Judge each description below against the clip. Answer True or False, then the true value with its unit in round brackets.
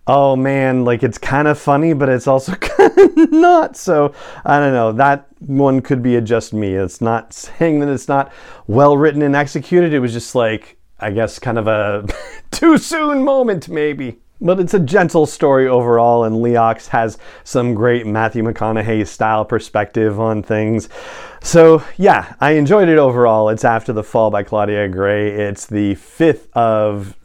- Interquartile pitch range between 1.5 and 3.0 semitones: False (5.2 semitones)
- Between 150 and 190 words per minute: True (180 wpm)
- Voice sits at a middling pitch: False (125 Hz)